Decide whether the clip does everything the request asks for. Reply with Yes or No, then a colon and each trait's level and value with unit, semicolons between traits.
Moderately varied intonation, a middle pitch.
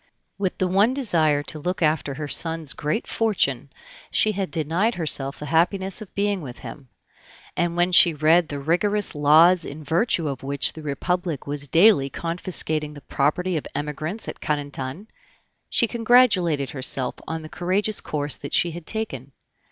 Yes: average, 4.2 semitones; medium, 160 Hz